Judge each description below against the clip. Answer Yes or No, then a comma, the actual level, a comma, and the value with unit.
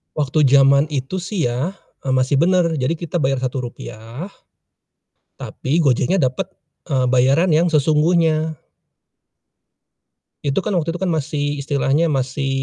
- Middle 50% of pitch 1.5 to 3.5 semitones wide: No, average, 4.0 semitones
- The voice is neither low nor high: Yes, medium, 145 Hz